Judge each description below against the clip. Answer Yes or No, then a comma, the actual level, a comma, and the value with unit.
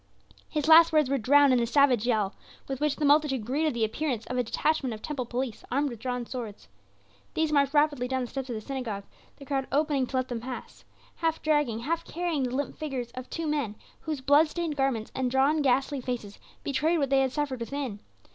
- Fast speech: Yes, fast, 215 wpm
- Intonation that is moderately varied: Yes, average, 3.2 semitones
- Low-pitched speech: No, very high, 270 Hz